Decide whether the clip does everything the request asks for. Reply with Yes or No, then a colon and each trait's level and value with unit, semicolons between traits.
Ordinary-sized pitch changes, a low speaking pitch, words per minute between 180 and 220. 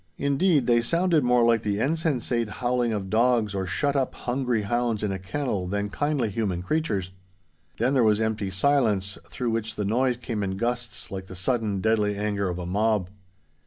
Yes: average, 3.7 semitones; low, 115 Hz; average, 185 wpm